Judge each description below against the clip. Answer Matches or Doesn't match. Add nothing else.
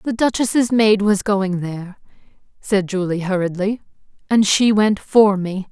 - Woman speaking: Matches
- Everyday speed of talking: Matches